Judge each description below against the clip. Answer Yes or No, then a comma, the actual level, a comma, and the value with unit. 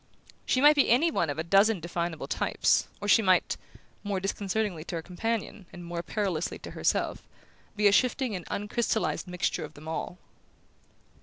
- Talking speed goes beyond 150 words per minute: Yes, average, 170 wpm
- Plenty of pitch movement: No, average, 4.3 semitones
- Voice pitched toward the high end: Yes, high, 195 Hz